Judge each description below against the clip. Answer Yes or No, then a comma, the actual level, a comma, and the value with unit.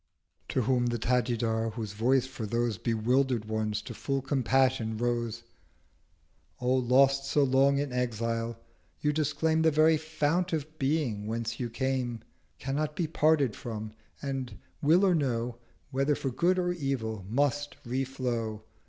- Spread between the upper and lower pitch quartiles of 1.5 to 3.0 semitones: No, average, 3.8 semitones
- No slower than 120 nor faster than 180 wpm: Yes, average, 155 wpm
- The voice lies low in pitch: Yes, low, 130 Hz